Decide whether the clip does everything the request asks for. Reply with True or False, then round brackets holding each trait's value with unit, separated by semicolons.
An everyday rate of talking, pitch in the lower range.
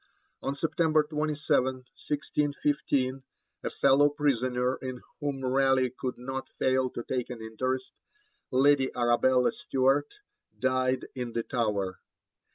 False (115 wpm; 130 Hz)